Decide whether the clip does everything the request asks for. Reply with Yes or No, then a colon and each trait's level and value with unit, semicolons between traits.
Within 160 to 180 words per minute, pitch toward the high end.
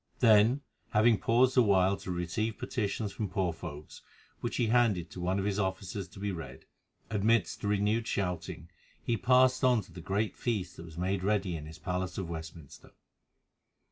No: average, 175 wpm; low, 100 Hz